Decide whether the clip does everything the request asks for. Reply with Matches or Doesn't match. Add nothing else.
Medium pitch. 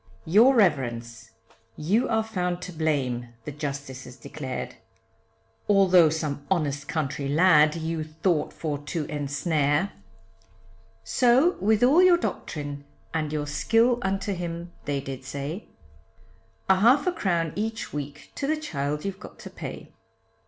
Matches